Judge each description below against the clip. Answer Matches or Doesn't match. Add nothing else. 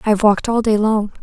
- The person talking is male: Doesn't match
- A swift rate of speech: Matches